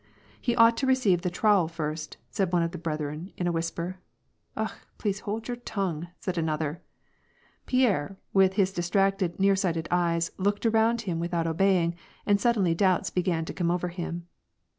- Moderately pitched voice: Yes, medium, 180 Hz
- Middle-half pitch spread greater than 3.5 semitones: No, average, 3.1 semitones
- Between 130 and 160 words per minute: No, average, 180 wpm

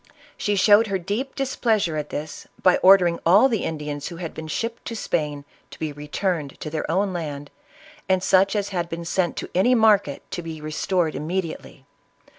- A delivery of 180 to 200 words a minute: Yes, average, 190 wpm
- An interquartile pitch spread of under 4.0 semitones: No, average, 4.5 semitones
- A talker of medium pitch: Yes, medium, 175 Hz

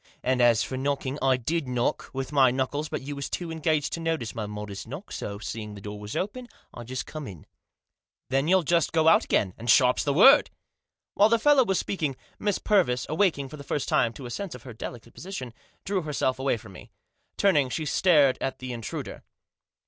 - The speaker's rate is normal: No, fast, 215 wpm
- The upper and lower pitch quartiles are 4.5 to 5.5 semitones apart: Yes, average, 5.2 semitones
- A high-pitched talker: No, low, 135 Hz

